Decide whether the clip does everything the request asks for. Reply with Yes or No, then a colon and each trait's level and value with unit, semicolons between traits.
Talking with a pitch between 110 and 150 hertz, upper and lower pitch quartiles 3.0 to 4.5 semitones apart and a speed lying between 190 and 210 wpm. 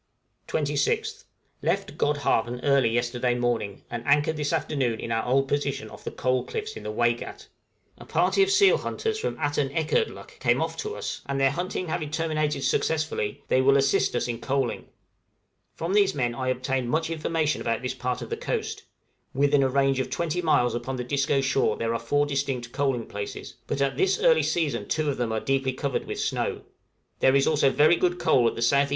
Yes: low, 135 Hz; average, 3.8 semitones; average, 200 wpm